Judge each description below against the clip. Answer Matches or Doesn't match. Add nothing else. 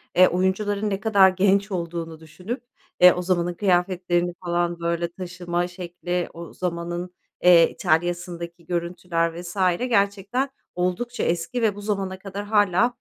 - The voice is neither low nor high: Matches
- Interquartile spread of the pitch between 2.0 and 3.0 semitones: Matches